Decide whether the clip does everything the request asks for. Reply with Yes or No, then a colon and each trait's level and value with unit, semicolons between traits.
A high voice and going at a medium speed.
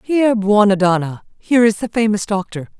Yes: high, 210 Hz; average, 170 wpm